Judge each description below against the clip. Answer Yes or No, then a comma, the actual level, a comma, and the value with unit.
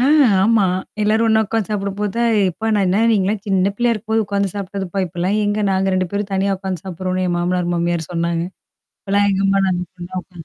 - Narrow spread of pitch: Yes, narrow, 2.2 semitones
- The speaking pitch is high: Yes, high, 195 Hz